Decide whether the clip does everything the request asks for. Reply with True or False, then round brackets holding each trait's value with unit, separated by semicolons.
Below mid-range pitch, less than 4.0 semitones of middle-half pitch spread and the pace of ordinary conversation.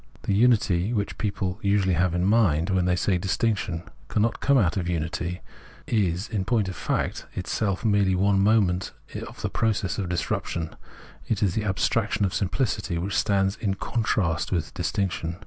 True (95 Hz; 2.8 semitones; 175 wpm)